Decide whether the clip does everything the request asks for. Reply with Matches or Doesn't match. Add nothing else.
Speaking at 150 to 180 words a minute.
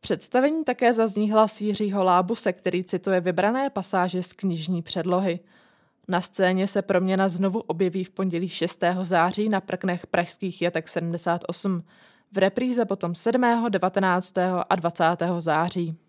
Doesn't match